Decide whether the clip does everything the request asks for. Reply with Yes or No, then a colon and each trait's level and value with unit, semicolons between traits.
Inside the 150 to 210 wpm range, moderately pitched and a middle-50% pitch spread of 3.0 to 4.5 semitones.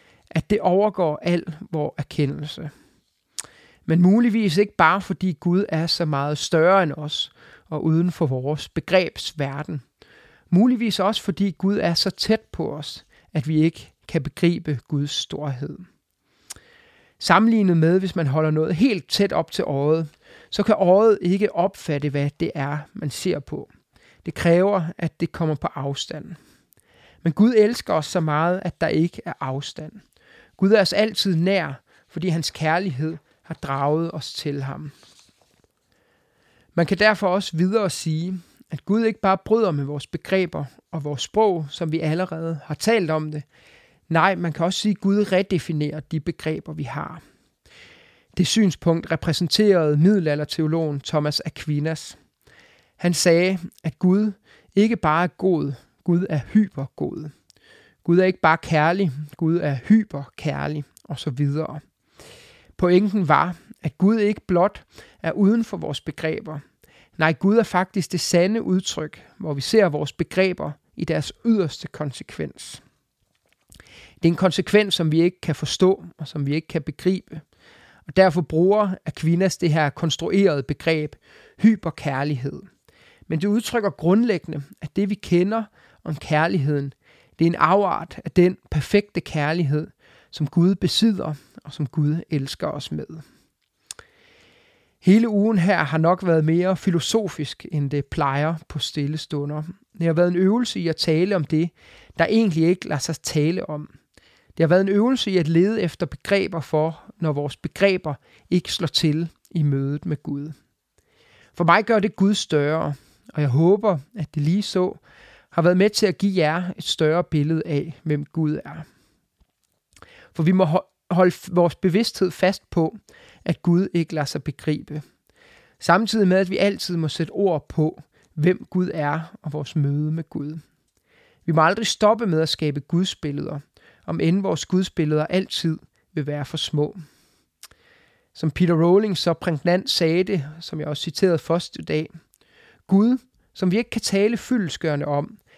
Yes: average, 160 wpm; medium, 170 Hz; average, 3.9 semitones